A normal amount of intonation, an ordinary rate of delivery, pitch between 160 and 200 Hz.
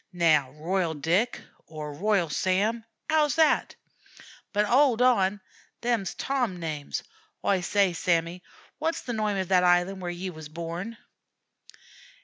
No: average, 4.8 semitones; slow, 130 wpm; high, 190 Hz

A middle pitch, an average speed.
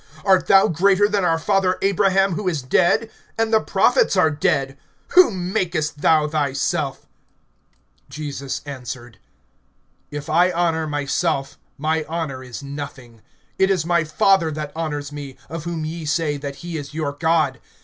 Yes: medium, 160 Hz; average, 150 wpm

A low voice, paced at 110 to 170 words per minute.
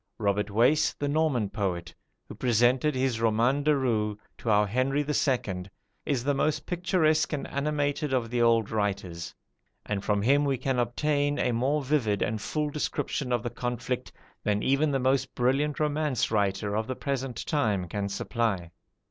Yes: low, 125 Hz; average, 165 wpm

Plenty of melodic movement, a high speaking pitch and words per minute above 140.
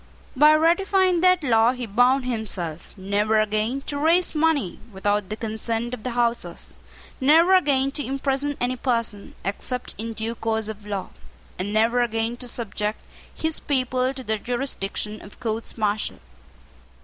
No: average, 4.2 semitones; high, 240 Hz; average, 150 wpm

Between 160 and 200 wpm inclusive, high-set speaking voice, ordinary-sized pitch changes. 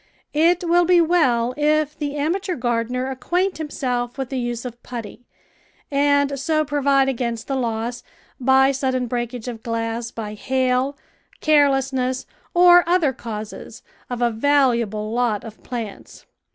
No: average, 140 wpm; very high, 260 Hz; average, 3.5 semitones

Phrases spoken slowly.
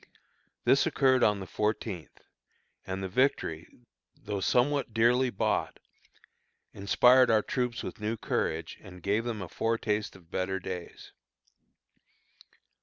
Yes: slow, 120 wpm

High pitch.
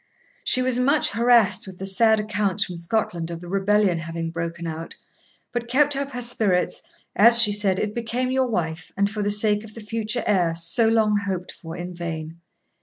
Yes: high, 205 Hz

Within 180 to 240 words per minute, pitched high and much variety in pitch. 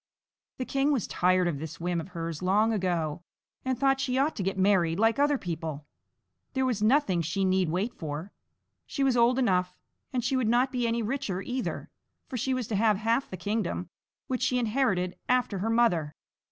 Yes: average, 195 wpm; high, 215 Hz; wide, 5.9 semitones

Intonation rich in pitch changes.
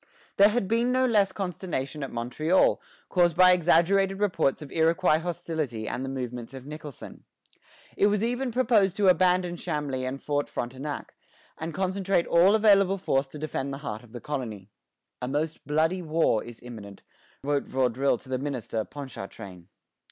Yes: wide, 6.1 semitones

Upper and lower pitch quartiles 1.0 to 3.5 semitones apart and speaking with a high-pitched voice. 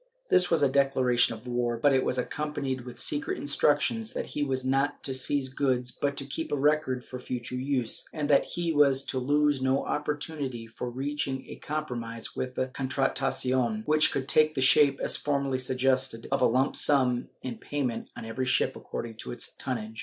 No: narrow, 2.4 semitones; low, 130 Hz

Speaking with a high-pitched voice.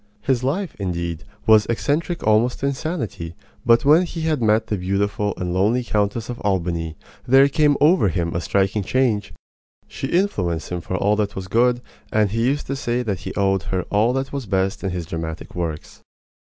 No: low, 105 Hz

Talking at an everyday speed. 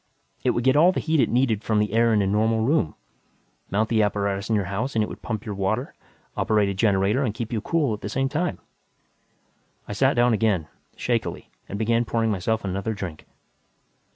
No: fast, 210 wpm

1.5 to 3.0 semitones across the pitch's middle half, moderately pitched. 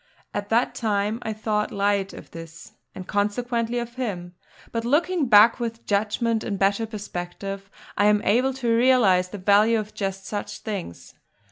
No: average, 2.7 semitones; high, 210 Hz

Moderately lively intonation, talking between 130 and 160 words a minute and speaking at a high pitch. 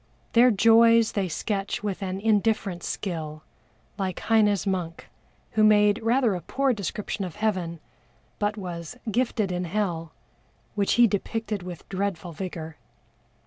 Yes: average, 3.5 semitones; slow, 135 wpm; high, 200 Hz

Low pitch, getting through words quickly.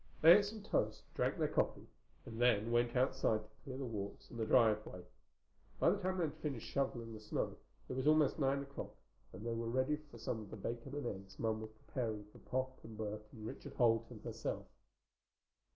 Yes: low, 120 Hz; fast, 210 wpm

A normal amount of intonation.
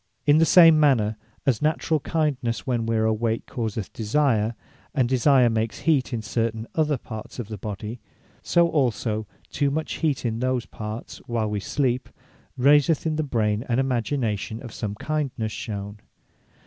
Yes: average, 4.6 semitones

